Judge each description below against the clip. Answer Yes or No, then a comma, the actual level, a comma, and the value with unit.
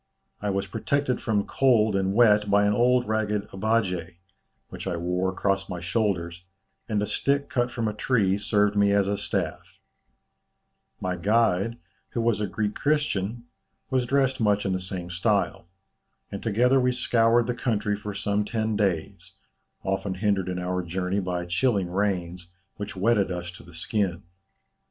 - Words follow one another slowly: No, average, 165 wpm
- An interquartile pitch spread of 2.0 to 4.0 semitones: Yes, average, 3.5 semitones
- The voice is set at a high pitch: No, low, 105 Hz